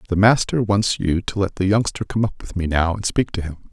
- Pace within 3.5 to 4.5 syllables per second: No, 5.6 syllables/s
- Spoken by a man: Yes, male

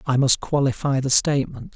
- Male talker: Yes, male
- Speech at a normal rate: Yes, average, 170 wpm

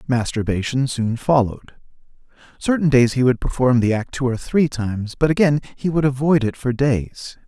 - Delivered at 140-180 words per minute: Yes, average, 175 wpm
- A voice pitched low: Yes, low, 130 Hz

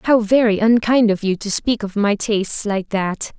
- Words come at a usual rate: No, fast, 215 wpm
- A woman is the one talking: Yes, female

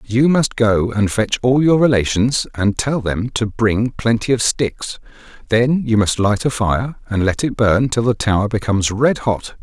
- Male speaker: Yes, male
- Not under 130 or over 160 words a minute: No, average, 200 wpm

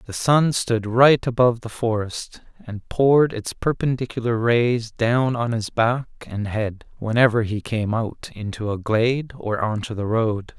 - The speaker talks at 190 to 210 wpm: No, average, 165 wpm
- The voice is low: Yes, low, 115 Hz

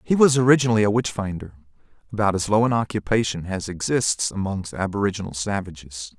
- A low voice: Yes, low, 105 Hz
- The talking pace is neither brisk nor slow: Yes, average, 145 wpm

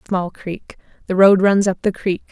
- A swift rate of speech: No, average, 180 wpm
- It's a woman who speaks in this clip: Yes, female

